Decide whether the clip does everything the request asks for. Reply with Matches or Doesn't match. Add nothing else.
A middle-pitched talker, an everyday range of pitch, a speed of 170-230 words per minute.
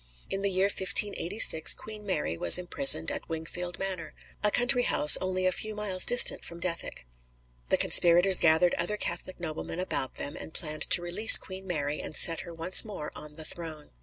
Matches